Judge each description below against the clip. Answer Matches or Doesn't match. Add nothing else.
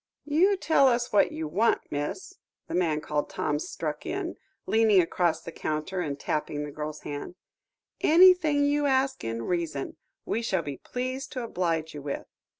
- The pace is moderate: Matches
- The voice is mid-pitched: Matches